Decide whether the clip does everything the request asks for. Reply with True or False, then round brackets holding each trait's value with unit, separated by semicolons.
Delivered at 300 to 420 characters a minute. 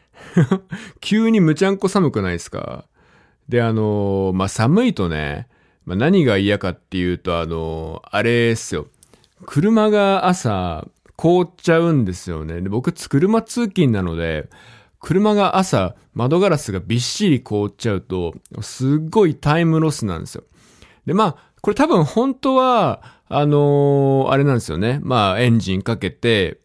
False (275 characters per minute)